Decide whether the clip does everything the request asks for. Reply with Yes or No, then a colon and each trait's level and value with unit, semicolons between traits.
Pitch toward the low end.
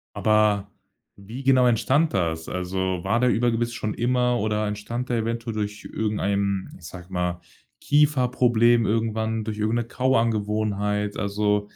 Yes: low, 110 Hz